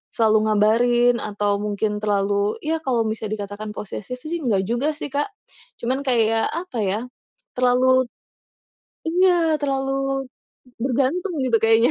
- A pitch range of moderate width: Yes, average, 4.2 semitones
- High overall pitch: Yes, high, 240 Hz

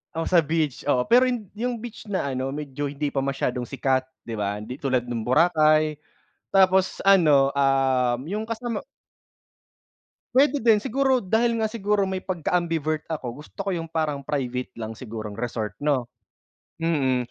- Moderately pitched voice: Yes, medium, 150 Hz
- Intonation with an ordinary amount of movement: No, wide, 6.8 semitones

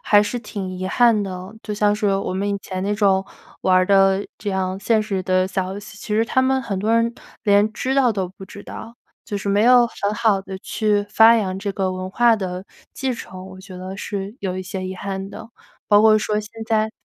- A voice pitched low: No, high, 200 Hz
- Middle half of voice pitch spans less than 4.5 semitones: Yes, narrow, 2.4 semitones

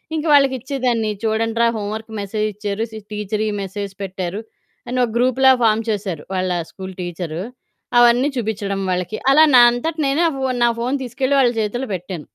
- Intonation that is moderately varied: Yes, average, 4.0 semitones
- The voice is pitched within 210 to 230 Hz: Yes, high, 220 Hz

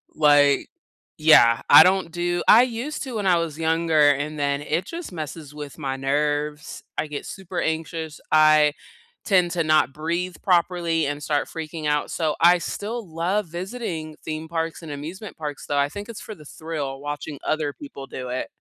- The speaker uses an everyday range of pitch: Yes, average, 3.0 semitones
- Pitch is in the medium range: Yes, medium, 160 Hz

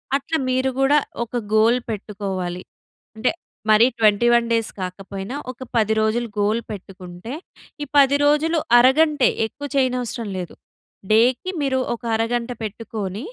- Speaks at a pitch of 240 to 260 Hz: No, high, 230 Hz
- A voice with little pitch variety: No, average, 3.8 semitones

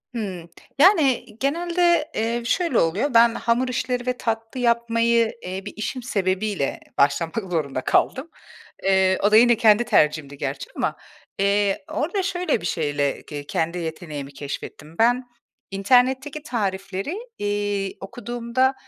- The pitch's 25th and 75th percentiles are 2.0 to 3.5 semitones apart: No, wide, 5.5 semitones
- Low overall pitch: No, high, 220 Hz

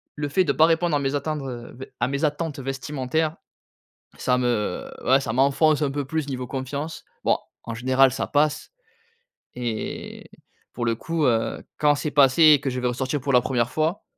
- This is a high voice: No, medium, 140 Hz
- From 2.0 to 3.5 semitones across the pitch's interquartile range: Yes, average, 3.1 semitones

